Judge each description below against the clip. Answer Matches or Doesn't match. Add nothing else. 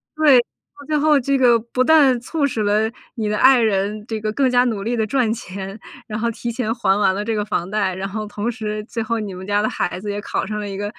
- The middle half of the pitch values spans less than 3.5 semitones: Matches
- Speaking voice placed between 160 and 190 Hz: Doesn't match